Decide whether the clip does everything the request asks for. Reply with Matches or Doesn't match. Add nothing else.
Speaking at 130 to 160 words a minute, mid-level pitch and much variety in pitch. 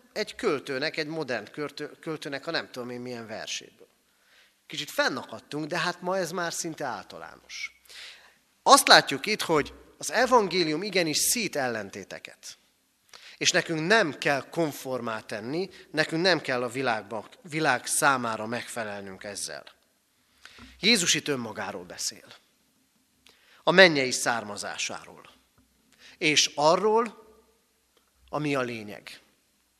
Doesn't match